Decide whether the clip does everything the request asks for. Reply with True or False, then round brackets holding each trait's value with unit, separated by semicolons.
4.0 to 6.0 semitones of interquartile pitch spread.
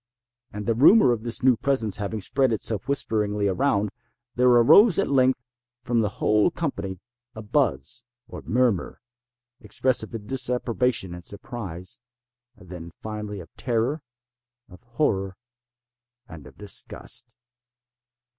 False (3.6 semitones)